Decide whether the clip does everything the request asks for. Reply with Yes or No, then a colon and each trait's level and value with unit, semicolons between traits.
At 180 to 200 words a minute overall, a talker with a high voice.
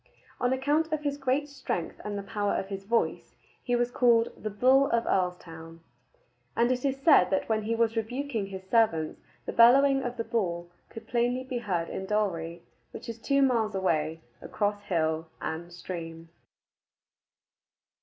No: average, 165 wpm; high, 220 Hz